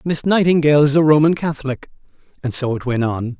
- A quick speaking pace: No, average, 195 wpm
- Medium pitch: Yes, medium, 145 Hz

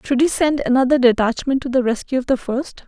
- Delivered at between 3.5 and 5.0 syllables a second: No, 5.8 syllables/s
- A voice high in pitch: Yes, very high, 260 Hz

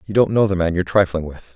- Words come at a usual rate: No, fast, 310 wpm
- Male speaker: Yes, male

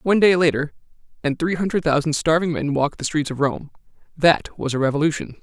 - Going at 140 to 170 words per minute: No, average, 200 wpm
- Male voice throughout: Yes, male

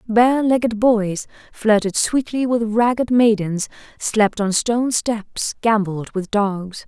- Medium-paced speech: No, slow, 130 wpm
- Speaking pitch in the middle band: No, high, 220 Hz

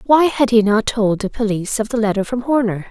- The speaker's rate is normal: No, fast, 250 wpm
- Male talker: No, female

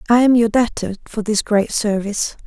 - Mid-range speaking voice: No, high, 220 Hz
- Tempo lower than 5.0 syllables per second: No, 5.3 syllables/s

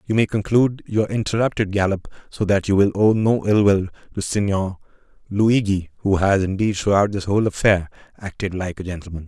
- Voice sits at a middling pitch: No, low, 100 Hz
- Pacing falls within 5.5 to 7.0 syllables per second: Yes, 5.6 syllables/s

